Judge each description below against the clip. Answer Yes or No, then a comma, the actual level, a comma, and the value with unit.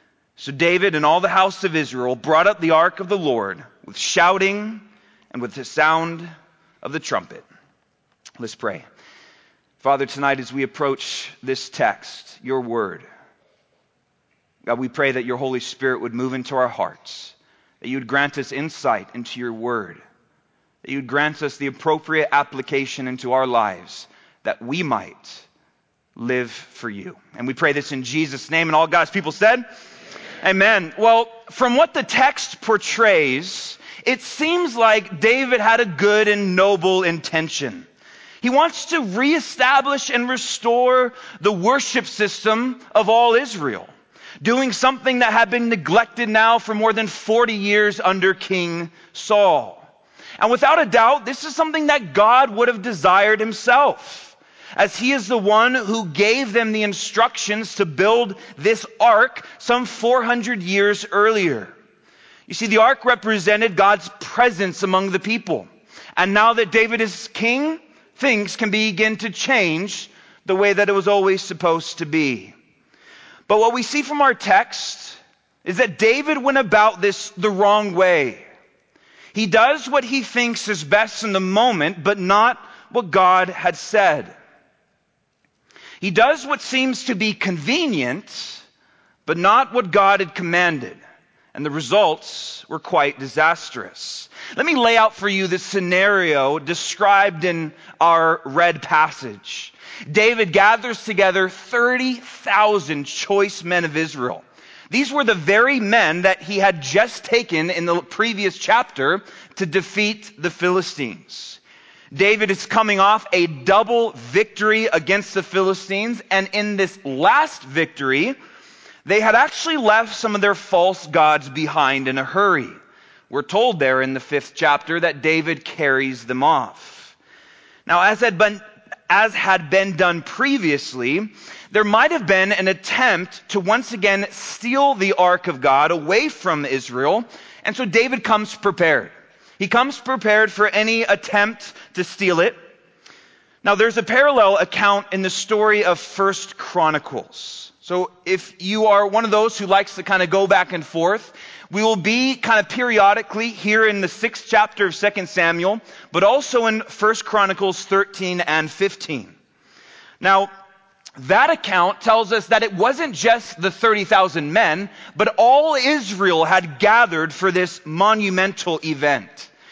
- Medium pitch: No, high, 200 Hz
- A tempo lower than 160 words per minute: Yes, average, 150 wpm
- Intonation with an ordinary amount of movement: Yes, average, 5.0 semitones